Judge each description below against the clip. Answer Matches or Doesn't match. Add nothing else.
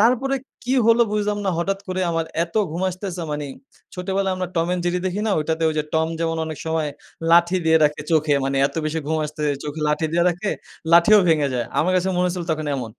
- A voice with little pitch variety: Doesn't match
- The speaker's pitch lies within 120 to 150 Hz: Doesn't match